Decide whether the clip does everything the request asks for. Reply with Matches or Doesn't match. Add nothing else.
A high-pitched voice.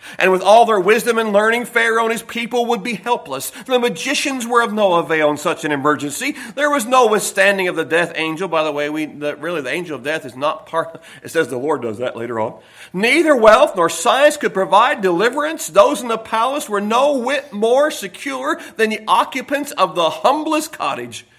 Matches